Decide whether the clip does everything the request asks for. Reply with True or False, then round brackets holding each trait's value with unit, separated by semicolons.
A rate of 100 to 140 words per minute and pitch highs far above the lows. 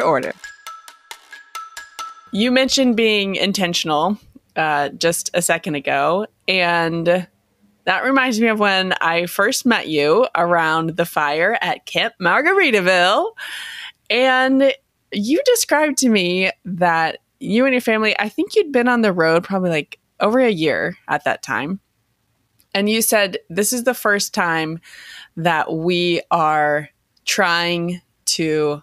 True (135 wpm; 7.2 semitones)